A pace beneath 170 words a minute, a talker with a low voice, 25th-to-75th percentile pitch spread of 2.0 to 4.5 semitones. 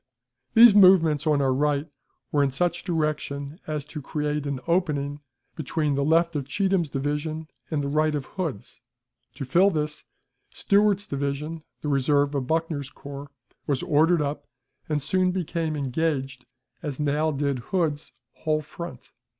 No: average, 150 wpm; medium, 150 Hz; narrow, 2.6 semitones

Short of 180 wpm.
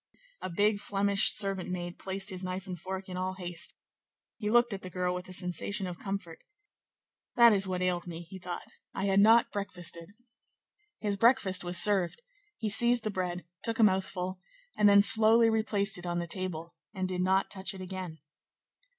No: average, 185 wpm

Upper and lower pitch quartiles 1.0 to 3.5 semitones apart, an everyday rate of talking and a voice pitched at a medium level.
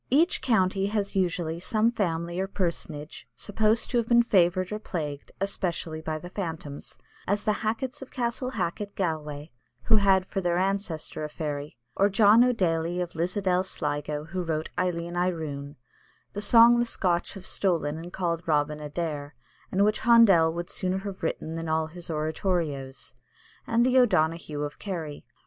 No: average, 4.3 semitones; average, 165 wpm; medium, 175 Hz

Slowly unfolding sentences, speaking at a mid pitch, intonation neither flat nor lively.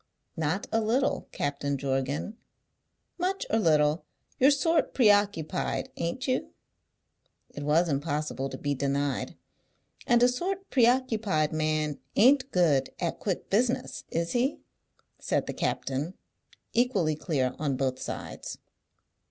No: slow, 120 wpm; medium, 170 Hz; wide, 9.0 semitones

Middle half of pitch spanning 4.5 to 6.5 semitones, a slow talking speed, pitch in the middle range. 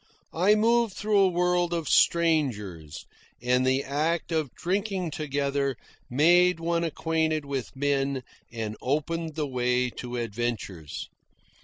Yes: average, 5.1 semitones; slow, 125 wpm; medium, 150 Hz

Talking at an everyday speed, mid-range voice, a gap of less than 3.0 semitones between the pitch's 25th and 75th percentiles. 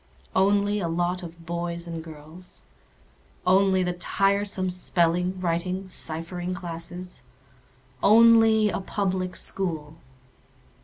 No: slow, 90 wpm; medium, 180 Hz; narrow, 2.4 semitones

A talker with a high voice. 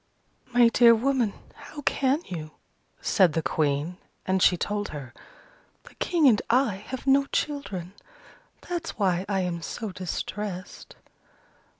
Yes: high, 205 Hz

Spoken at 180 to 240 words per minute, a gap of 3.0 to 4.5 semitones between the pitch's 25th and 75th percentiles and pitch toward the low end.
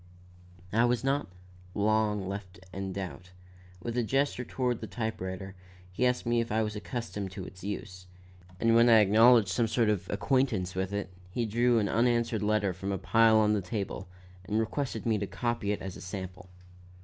Yes: average, 190 wpm; average, 3.4 semitones; low, 105 Hz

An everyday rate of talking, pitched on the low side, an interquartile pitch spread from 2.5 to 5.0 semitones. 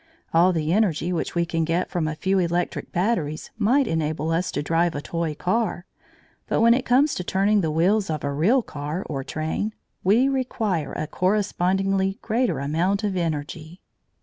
No: average, 175 wpm; medium, 175 Hz; average, 4.4 semitones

